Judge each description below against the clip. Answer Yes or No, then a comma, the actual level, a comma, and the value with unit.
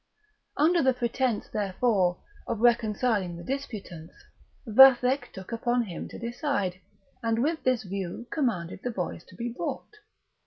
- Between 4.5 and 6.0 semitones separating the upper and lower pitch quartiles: Yes, average, 5.0 semitones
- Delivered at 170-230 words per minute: No, average, 140 wpm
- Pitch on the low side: No, high, 235 Hz